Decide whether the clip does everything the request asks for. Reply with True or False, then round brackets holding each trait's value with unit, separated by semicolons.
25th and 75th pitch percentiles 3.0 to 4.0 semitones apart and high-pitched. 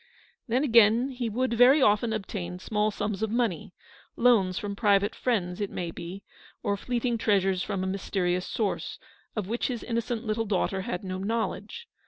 True (3.4 semitones; 210 Hz)